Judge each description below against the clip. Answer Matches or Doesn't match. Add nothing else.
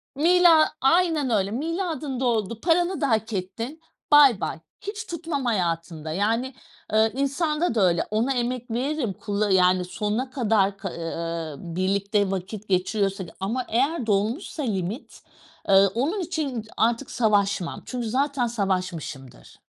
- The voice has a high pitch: Matches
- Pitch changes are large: Matches